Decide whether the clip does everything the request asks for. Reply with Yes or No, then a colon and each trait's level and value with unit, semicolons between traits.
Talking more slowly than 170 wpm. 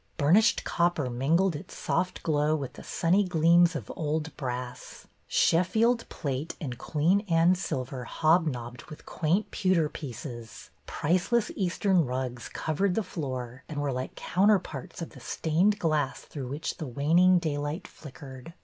Yes: average, 140 wpm